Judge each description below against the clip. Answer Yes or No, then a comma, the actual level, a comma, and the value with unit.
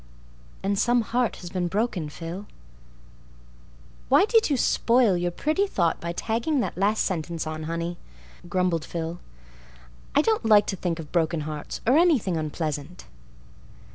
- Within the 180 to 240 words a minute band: No, average, 140 wpm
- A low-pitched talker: No, medium, 180 Hz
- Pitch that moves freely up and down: Yes, wide, 5.9 semitones